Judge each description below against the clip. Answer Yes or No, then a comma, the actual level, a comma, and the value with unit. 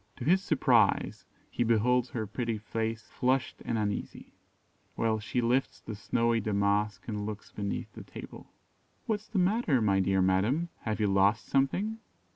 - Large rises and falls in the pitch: No, average, 3.9 semitones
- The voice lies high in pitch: No, low, 115 Hz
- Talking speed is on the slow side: No, average, 160 wpm